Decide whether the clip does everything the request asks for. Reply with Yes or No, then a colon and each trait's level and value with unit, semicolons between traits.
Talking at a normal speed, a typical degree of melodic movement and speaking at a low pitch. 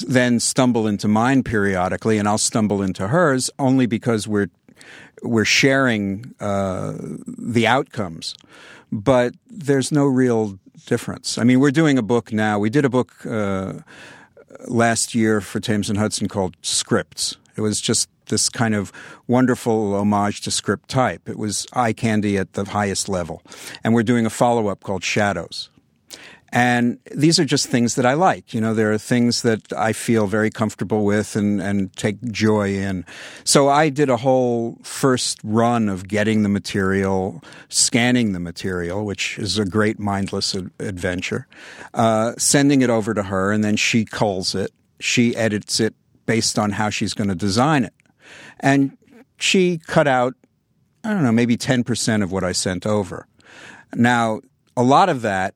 Yes: average, 165 wpm; average, 3.4 semitones; low, 110 Hz